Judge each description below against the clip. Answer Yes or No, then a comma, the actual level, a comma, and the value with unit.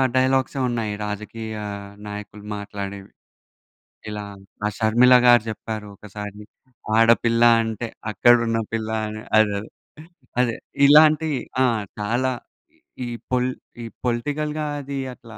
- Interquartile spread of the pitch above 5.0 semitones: No, average, 2.9 semitones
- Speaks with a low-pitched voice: Yes, low, 115 Hz